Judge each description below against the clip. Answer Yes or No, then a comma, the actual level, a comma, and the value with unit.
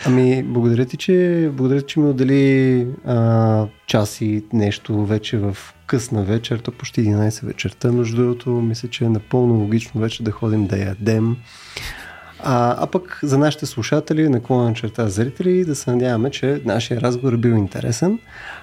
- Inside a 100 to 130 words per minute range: No, average, 160 wpm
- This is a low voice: Yes, low, 120 Hz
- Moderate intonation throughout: Yes, average, 3.2 semitones